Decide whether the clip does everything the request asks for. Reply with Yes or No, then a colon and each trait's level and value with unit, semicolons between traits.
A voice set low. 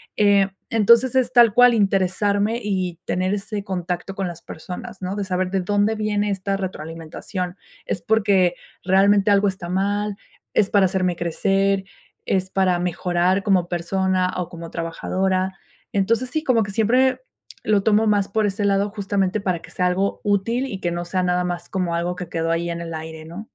No: high, 195 Hz